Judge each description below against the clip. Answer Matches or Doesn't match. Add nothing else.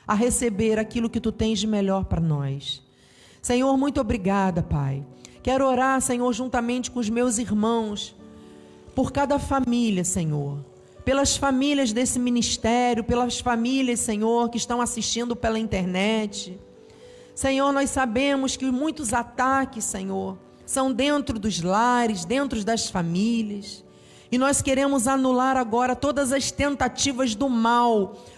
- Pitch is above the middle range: Matches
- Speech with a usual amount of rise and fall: Matches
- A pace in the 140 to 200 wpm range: Doesn't match